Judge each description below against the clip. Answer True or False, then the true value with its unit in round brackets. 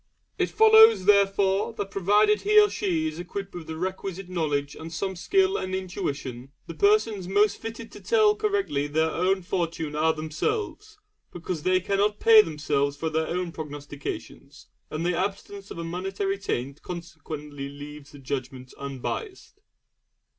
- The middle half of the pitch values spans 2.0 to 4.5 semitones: False (5.1 semitones)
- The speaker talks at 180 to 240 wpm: False (155 wpm)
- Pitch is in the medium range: True (180 Hz)